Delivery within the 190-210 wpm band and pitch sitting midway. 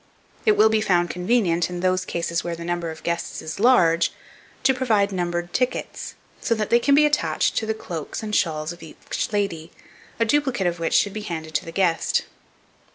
Yes: average, 200 wpm; medium, 180 Hz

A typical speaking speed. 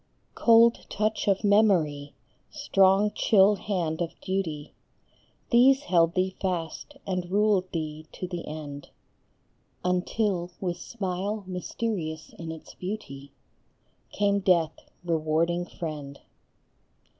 No: slow, 110 wpm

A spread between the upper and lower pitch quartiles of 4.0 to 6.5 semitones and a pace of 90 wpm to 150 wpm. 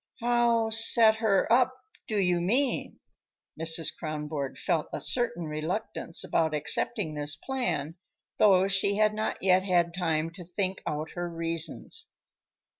Yes: average, 5.2 semitones; slow, 135 wpm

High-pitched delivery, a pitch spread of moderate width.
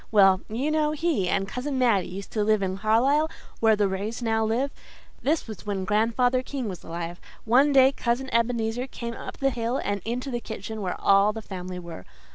Yes: high, 225 Hz; average, 4.3 semitones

